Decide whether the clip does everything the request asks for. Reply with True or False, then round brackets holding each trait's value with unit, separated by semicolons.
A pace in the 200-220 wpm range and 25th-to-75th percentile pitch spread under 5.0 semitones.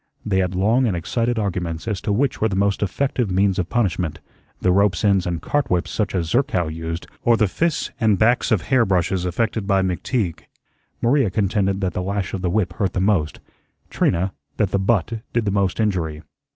True (205 wpm; 3.5 semitones)